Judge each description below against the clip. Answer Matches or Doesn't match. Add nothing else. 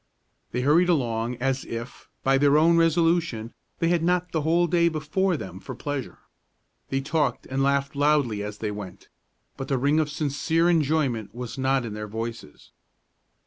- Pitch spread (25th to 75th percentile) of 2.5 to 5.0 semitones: Doesn't match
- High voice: Doesn't match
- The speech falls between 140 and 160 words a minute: Doesn't match